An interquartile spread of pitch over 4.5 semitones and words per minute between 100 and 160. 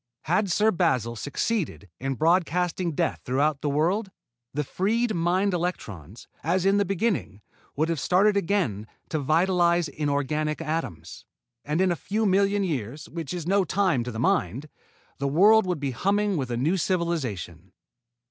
Yes: wide, 5.4 semitones; average, 155 wpm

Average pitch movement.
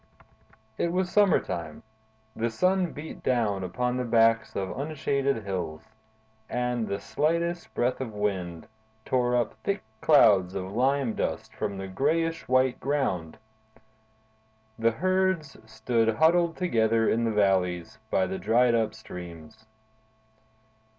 No: wide, 6.5 semitones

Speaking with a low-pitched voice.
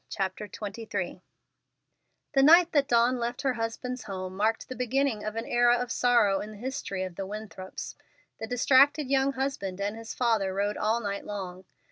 No: high, 225 Hz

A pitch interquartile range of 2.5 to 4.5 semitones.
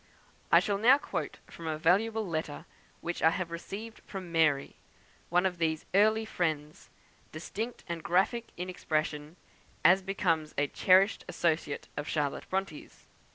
Yes: average, 3.8 semitones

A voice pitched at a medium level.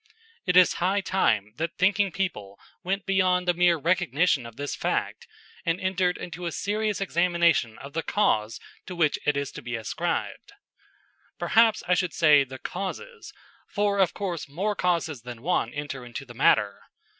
Yes: medium, 175 Hz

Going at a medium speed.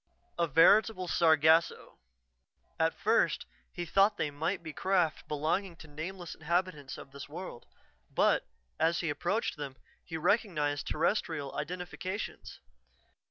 No: slow, 120 wpm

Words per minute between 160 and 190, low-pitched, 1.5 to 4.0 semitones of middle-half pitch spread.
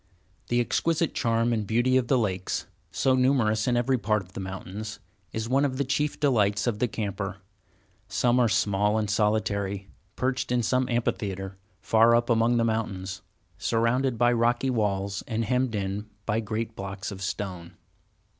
Yes: average, 165 wpm; low, 110 Hz; average, 3.3 semitones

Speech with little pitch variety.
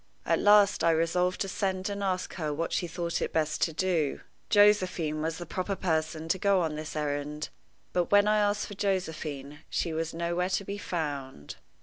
No: average, 3.6 semitones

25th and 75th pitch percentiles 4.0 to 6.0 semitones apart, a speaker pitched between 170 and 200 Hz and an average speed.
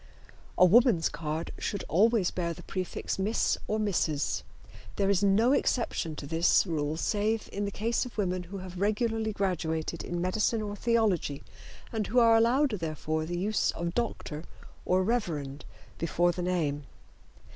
Yes: average, 4.6 semitones; medium, 185 Hz; average, 155 wpm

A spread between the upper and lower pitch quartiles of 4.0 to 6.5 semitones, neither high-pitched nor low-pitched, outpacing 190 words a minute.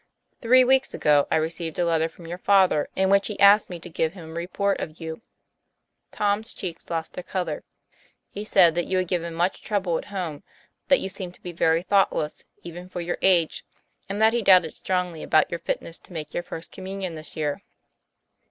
No: average, 3.0 semitones; medium, 175 Hz; fast, 205 wpm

